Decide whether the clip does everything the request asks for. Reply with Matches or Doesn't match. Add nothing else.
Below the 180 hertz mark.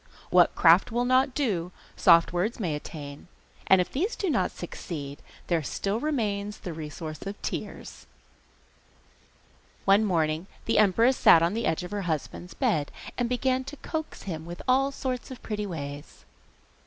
Doesn't match